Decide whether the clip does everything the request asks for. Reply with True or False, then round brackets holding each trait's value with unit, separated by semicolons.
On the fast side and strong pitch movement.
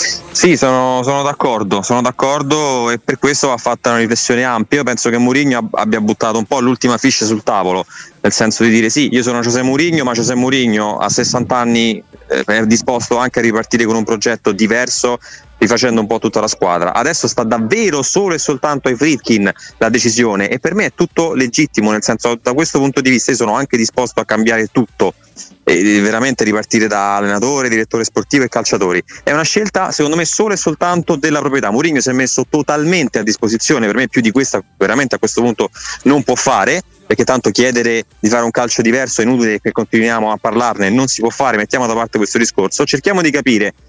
False (205 wpm; 2.9 semitones)